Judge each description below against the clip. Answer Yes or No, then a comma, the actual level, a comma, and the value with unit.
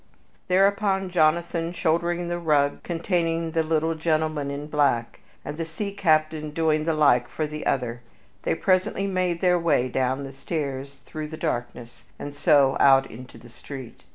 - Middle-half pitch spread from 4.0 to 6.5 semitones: No, average, 3.4 semitones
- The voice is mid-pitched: Yes, medium, 155 Hz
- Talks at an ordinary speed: Yes, average, 160 wpm